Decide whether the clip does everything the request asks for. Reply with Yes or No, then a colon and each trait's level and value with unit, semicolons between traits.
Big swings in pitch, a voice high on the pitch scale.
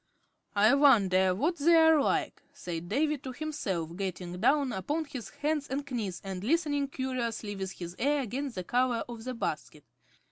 Yes: wide, 6.9 semitones; very high, 250 Hz